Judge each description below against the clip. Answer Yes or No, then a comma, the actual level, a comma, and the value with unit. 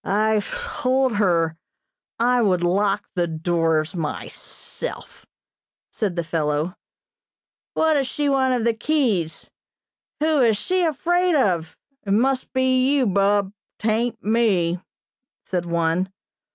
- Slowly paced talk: Yes, slow, 115 wpm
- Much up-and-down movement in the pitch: Yes, wide, 7.0 semitones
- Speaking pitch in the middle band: No, high, 210 Hz